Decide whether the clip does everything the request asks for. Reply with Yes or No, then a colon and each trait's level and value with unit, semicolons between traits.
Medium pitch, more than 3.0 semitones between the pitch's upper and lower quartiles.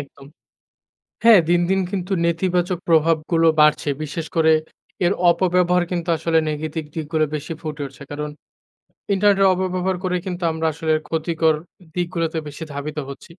No: medium, 165 Hz; narrow, 2.5 semitones